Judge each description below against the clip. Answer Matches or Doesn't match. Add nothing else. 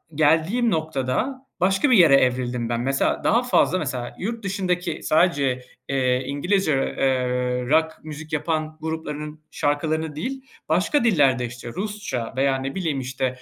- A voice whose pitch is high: Doesn't match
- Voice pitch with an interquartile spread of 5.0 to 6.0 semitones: Matches